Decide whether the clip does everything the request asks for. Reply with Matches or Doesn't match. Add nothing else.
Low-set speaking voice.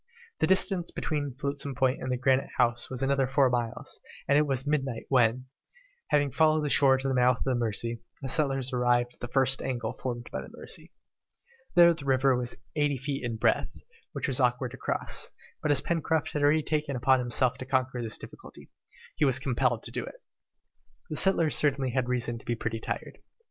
Matches